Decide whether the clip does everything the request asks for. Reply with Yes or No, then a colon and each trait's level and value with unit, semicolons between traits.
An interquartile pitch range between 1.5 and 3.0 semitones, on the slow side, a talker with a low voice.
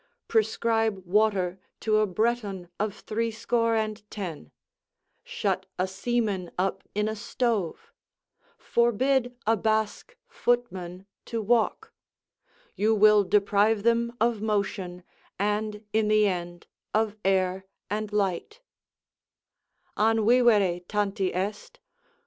No: average, 2.7 semitones; slow, 110 wpm; high, 210 Hz